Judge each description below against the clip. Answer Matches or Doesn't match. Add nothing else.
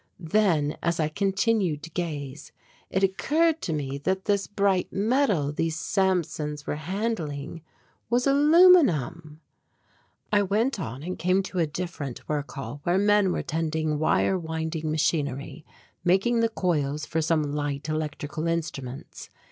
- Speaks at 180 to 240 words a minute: Doesn't match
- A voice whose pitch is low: Doesn't match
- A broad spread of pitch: Doesn't match